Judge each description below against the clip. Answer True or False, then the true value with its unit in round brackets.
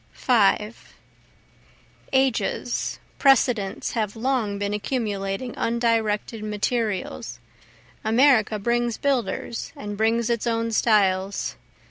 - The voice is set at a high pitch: True (225 Hz)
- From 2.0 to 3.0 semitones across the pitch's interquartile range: True (2.5 semitones)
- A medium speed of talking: False (85 wpm)